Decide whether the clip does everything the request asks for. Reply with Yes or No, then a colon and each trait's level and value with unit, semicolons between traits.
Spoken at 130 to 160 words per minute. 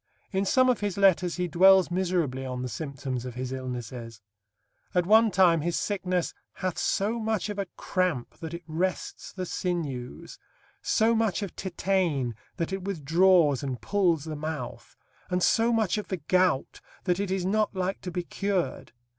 No: average, 170 wpm